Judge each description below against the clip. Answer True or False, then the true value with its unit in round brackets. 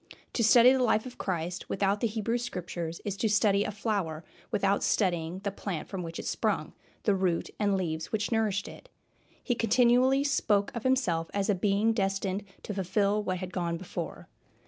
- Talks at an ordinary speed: True (185 wpm)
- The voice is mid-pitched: False (200 Hz)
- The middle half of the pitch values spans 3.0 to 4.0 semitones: True (3.4 semitones)